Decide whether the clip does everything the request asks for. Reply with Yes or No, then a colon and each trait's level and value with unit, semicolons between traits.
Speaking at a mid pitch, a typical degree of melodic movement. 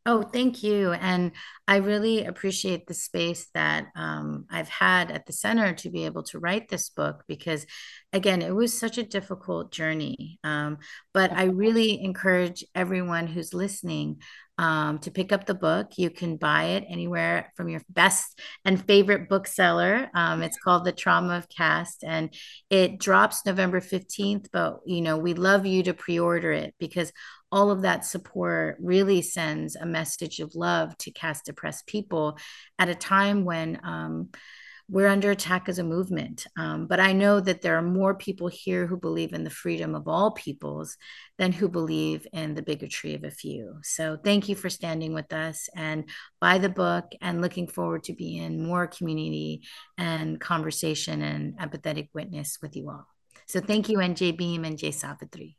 Yes: medium, 175 Hz; average, 3.5 semitones